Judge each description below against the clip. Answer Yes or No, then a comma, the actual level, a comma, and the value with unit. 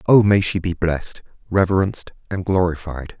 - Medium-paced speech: Yes, average, 150 wpm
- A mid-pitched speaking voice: No, very low, 90 Hz